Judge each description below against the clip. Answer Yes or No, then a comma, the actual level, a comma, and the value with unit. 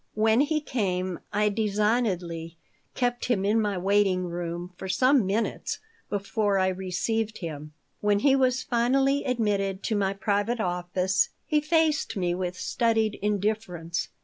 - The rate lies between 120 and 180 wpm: Yes, average, 140 wpm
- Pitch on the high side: Yes, high, 205 Hz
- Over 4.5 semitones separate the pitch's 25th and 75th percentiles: No, average, 4.0 semitones